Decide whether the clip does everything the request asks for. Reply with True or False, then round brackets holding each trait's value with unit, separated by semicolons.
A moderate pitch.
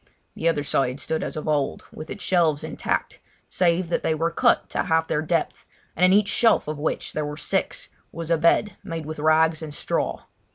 True (160 Hz)